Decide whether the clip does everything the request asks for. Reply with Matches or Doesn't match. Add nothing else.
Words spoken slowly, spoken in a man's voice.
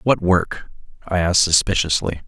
Matches